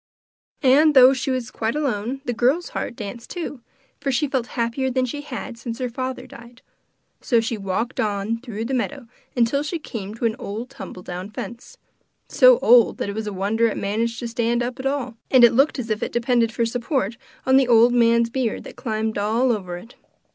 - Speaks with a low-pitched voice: No, high, 235 Hz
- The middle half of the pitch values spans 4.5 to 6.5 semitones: No, average, 2.7 semitones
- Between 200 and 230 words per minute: Yes, fast, 205 wpm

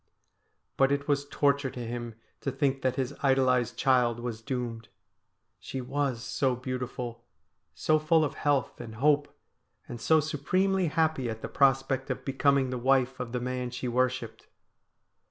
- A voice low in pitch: Yes, low, 130 Hz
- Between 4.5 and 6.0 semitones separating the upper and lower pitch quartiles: No, narrow, 2.5 semitones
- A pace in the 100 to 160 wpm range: Yes, average, 155 wpm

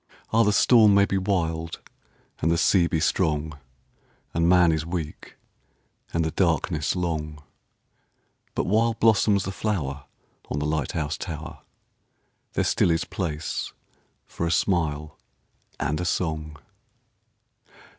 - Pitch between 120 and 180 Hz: No, very low, 85 Hz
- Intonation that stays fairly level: No, average, 3.5 semitones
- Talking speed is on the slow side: Yes, slow, 130 wpm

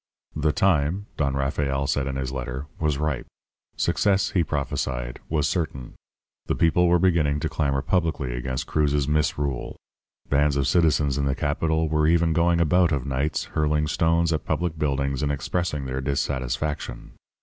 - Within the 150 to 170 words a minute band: Yes, average, 160 wpm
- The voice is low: Yes, very low, 75 Hz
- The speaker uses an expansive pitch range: No, average, 2.9 semitones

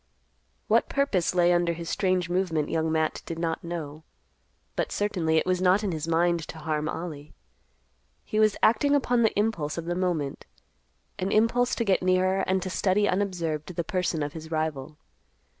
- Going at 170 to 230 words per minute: Yes, average, 175 wpm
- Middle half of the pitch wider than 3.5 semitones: No, average, 3.1 semitones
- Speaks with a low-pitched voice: No, medium, 175 Hz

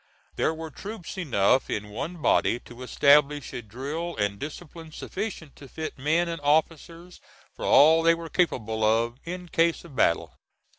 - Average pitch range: Yes, average, 4.8 semitones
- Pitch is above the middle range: No, medium, 155 Hz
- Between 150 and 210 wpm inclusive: Yes, average, 160 wpm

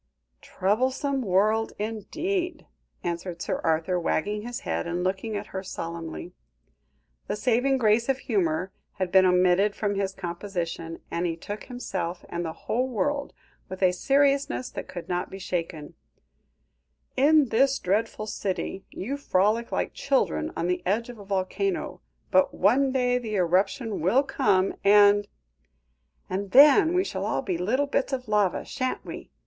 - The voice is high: Yes, high, 205 Hz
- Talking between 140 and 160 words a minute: Yes, average, 155 wpm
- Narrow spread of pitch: No, wide, 5.5 semitones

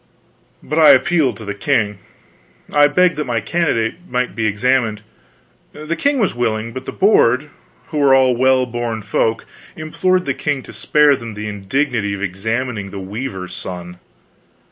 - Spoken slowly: No, average, 165 wpm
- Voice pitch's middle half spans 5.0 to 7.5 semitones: Yes, wide, 5.5 semitones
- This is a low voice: Yes, low, 125 Hz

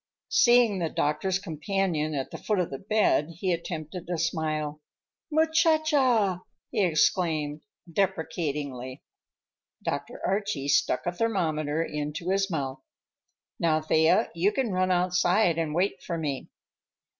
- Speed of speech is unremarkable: No, slow, 130 wpm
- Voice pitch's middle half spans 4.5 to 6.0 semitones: No, average, 4.1 semitones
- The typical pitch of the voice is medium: Yes, medium, 170 Hz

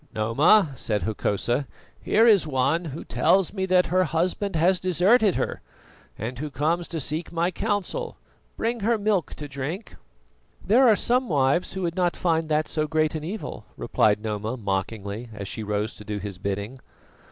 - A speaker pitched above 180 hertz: No, medium, 160 Hz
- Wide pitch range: Yes, wide, 8.3 semitones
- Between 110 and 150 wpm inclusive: No, average, 175 wpm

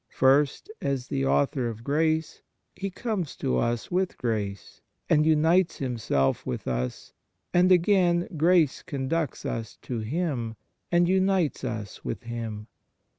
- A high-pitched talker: No, medium, 140 Hz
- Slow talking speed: Yes, slow, 130 wpm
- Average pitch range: No, wide, 7.3 semitones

